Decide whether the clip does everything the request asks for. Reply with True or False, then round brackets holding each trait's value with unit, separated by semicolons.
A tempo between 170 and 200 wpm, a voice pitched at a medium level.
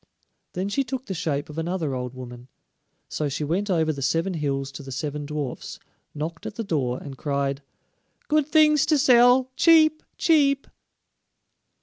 False (160 wpm; 160 Hz)